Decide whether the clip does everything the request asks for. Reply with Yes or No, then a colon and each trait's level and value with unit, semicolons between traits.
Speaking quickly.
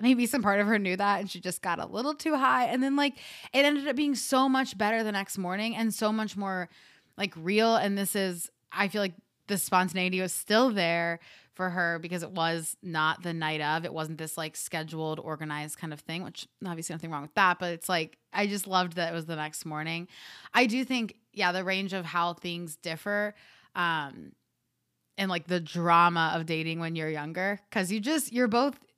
Yes: fast, 220 wpm